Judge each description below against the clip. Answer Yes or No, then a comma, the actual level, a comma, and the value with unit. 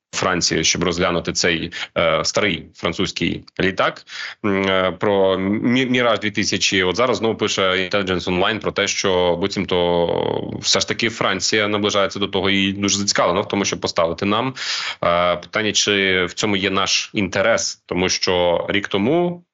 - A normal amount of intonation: No, narrow, 2.1 semitones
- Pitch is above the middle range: No, low, 100 Hz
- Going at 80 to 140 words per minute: No, fast, 155 wpm